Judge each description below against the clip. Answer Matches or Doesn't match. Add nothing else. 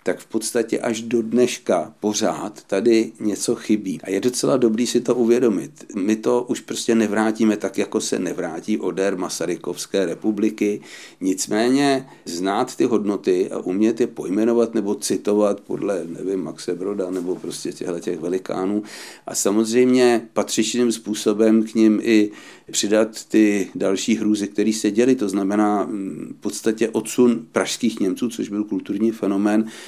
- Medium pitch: Doesn't match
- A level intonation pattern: Matches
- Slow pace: Doesn't match